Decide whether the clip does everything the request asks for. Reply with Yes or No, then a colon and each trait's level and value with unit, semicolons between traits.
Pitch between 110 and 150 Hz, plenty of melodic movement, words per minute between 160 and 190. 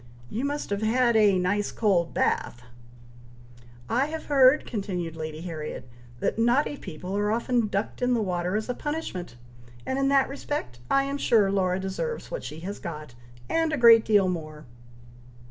No: high, 210 Hz; wide, 6.3 semitones; average, 170 wpm